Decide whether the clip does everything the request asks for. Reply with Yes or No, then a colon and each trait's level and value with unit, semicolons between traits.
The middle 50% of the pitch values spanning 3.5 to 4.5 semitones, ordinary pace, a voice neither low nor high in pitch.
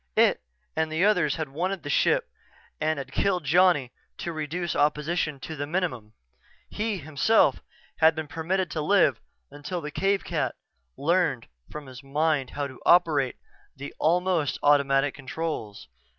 Yes: average, 3.9 semitones; average, 150 wpm; medium, 155 Hz